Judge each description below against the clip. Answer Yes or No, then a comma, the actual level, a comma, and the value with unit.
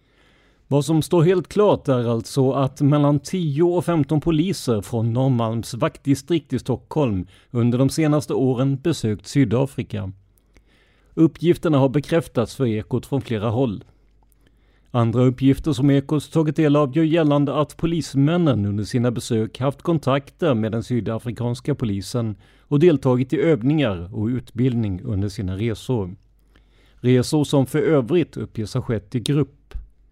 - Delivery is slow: No, average, 140 wpm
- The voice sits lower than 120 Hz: No, low, 130 Hz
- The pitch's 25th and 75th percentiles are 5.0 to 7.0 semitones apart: No, average, 4.5 semitones